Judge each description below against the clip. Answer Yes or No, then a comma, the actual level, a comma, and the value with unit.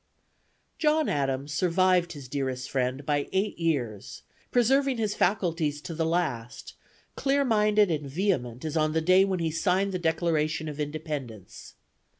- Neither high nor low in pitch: Yes, medium, 160 Hz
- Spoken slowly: No, average, 150 wpm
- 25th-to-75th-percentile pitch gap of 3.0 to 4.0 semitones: No, average, 5.0 semitones